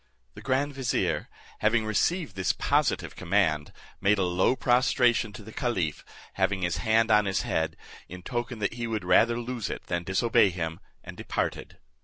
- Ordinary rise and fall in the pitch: Yes, average, 4.6 semitones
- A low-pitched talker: Yes, low, 110 Hz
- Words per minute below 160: No, average, 170 wpm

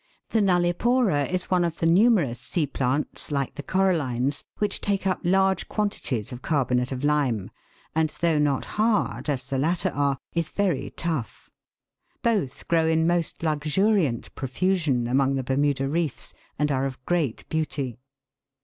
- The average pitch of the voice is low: No, medium, 155 Hz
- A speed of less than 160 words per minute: Yes, average, 150 wpm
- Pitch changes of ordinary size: Yes, average, 4.9 semitones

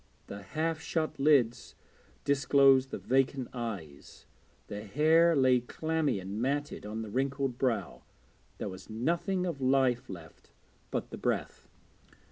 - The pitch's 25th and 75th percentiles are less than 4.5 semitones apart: No, average, 4.8 semitones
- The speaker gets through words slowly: Yes, slow, 130 wpm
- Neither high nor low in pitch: No, low, 130 Hz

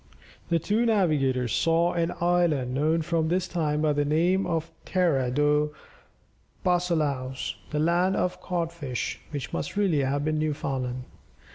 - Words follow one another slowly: No, average, 145 wpm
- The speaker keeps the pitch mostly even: No, average, 3.4 semitones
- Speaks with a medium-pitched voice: Yes, medium, 155 Hz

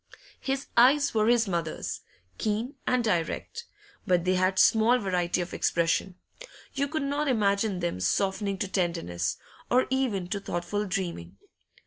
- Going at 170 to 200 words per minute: No, average, 140 wpm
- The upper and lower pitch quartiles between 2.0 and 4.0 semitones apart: No, wide, 5.5 semitones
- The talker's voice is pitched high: Yes, high, 200 Hz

